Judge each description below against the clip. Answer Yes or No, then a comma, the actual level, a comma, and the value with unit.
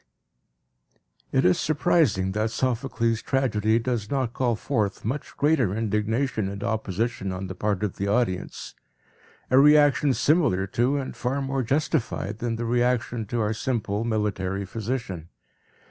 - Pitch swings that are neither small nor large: Yes, average, 4.2 semitones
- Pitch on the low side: Yes, low, 115 Hz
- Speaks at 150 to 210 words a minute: No, average, 140 wpm